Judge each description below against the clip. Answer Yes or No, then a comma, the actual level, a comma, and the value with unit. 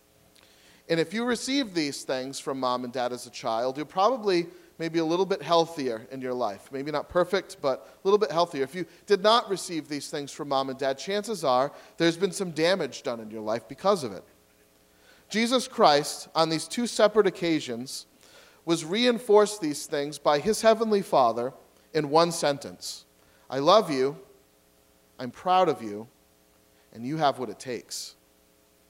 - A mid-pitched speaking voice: Yes, medium, 150 Hz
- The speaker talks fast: No, average, 180 wpm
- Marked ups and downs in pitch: Yes, wide, 7.5 semitones